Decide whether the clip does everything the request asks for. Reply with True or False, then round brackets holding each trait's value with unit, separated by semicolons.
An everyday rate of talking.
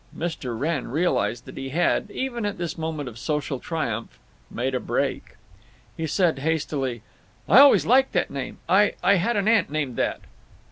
True (170 wpm)